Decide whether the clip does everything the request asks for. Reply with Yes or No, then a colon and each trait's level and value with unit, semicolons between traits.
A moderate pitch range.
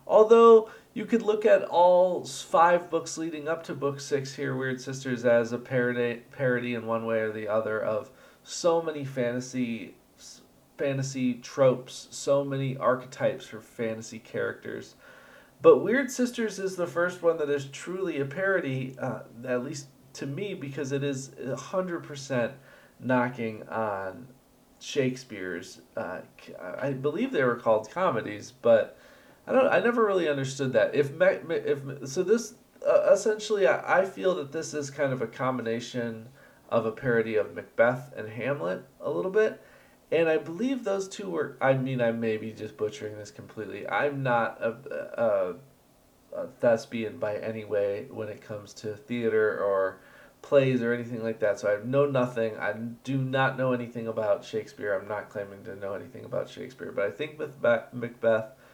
No: wide, 6.1 semitones